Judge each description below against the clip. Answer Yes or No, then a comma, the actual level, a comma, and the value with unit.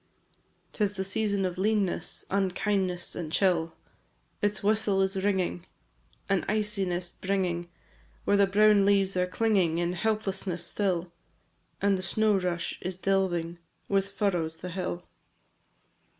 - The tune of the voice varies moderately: No, narrow, 2.2 semitones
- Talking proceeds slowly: Yes, slow, 130 wpm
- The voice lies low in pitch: No, high, 190 Hz